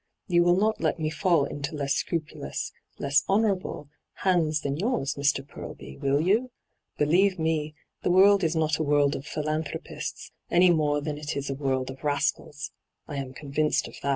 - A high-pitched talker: No, medium, 150 Hz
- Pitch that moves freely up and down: No, average, 3.5 semitones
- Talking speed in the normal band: Yes, average, 180 wpm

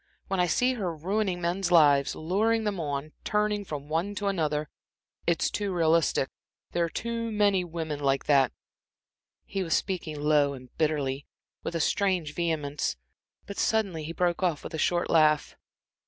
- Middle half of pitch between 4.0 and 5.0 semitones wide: Yes, average, 4.5 semitones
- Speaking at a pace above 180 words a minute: No, average, 165 wpm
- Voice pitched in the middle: Yes, medium, 170 Hz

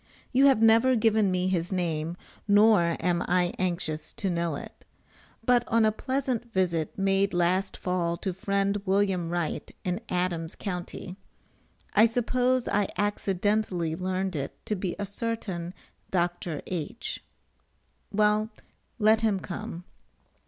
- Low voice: No, high, 190 Hz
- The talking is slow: Yes, slow, 130 wpm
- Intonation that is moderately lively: Yes, average, 3.6 semitones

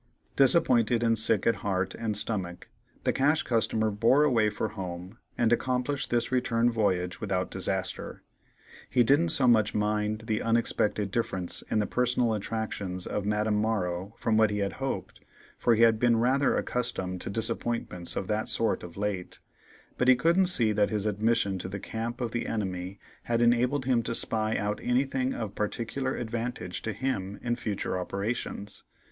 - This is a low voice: Yes, low, 110 Hz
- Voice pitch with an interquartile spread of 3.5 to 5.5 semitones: No, average, 3.0 semitones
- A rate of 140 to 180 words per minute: Yes, average, 170 wpm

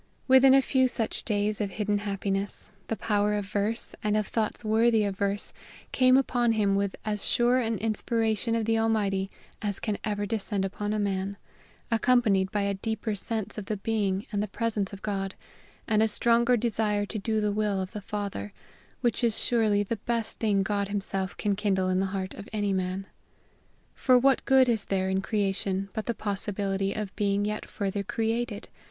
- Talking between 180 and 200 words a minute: Yes, average, 190 wpm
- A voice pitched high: Yes, high, 210 Hz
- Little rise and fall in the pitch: Yes, narrow, 2.2 semitones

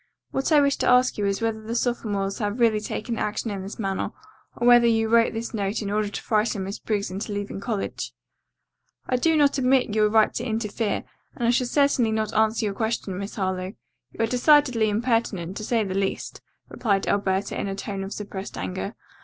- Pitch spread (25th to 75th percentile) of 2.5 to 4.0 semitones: Yes, average, 2.9 semitones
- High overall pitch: Yes, high, 220 Hz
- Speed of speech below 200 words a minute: No, fast, 205 wpm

